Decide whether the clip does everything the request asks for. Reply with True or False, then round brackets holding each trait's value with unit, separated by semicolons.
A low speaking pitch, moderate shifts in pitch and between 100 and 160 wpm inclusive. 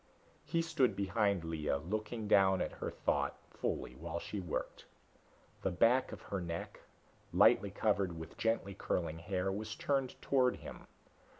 True (100 Hz; 4.8 semitones; 140 wpm)